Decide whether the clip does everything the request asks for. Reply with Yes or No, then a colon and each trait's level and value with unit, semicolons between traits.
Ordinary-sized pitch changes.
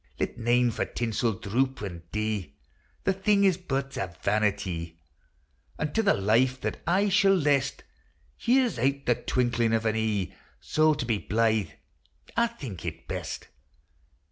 No: wide, 6.0 semitones